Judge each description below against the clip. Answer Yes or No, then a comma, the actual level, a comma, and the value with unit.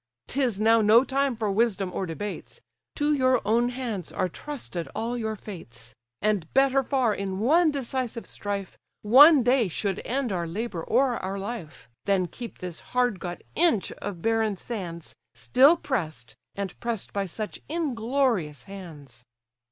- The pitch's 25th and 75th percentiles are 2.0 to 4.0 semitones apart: No, average, 5.3 semitones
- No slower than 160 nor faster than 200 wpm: No, average, 150 wpm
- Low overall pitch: No, high, 220 Hz